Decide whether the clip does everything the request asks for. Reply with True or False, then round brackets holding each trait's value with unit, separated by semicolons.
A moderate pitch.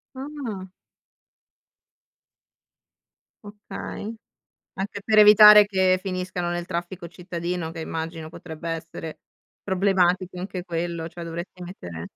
True (180 Hz)